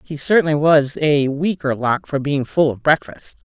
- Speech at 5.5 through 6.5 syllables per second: No, 4.6 syllables/s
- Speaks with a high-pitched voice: No, medium, 145 Hz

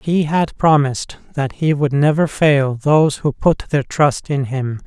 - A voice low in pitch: No, medium, 145 Hz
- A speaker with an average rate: Yes, average, 185 wpm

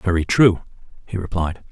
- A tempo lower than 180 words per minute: Yes, average, 140 wpm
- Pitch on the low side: Yes, very low, 90 Hz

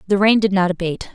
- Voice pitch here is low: No, high, 195 Hz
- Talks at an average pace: No, fast, 260 wpm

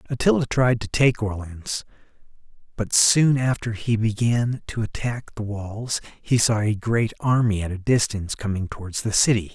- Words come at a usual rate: Yes, average, 165 wpm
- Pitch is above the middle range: No, low, 110 Hz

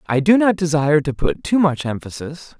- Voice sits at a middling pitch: Yes, medium, 160 Hz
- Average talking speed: No, fast, 210 wpm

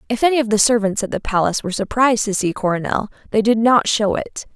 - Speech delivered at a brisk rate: Yes, fast, 235 wpm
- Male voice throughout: No, female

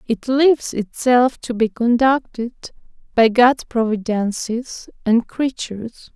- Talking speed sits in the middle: No, slow, 105 wpm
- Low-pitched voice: No, high, 240 Hz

